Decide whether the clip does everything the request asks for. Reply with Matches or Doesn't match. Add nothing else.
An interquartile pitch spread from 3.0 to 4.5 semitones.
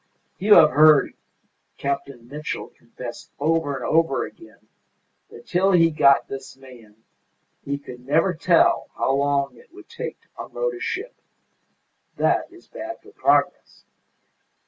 Doesn't match